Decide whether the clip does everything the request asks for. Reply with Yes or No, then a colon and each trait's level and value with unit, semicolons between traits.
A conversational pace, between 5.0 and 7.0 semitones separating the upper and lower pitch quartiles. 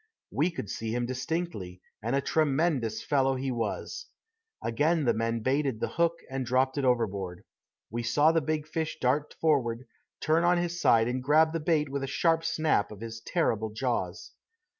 Yes: average, 180 wpm; average, 5.3 semitones